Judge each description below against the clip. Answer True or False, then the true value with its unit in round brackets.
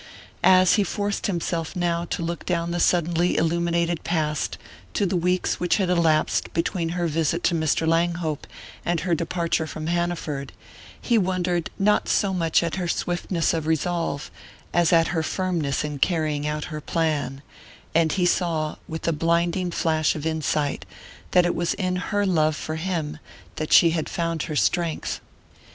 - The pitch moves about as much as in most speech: False (1.8 semitones)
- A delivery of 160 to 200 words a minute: True (165 wpm)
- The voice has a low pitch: False (170 Hz)